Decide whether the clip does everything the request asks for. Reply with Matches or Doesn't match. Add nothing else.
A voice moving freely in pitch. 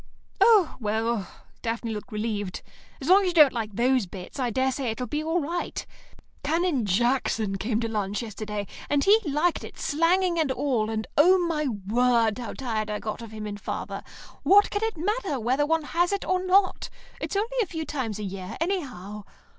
Matches